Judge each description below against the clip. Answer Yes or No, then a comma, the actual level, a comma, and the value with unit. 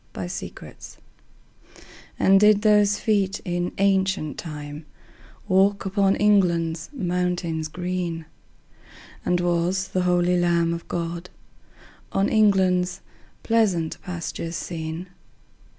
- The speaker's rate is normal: No, slow, 105 wpm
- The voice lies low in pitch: No, medium, 180 Hz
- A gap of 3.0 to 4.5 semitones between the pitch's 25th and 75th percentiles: No, narrow, 2.4 semitones